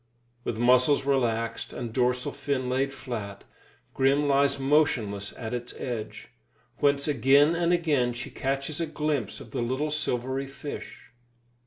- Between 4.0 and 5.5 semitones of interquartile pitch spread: No, average, 2.9 semitones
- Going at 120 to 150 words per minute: Yes, average, 140 wpm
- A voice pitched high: No, low, 135 Hz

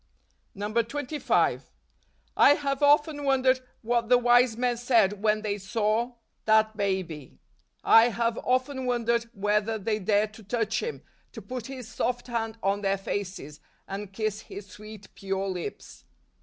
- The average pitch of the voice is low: No, high, 220 Hz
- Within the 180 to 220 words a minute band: No, average, 150 wpm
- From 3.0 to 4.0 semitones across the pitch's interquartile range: Yes, average, 3.3 semitones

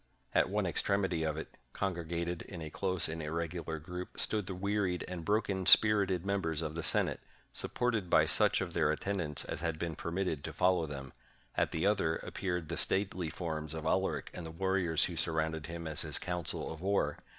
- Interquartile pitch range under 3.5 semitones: Yes, average, 2.9 semitones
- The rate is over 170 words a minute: Yes, average, 195 wpm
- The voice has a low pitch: Yes, very low, 85 Hz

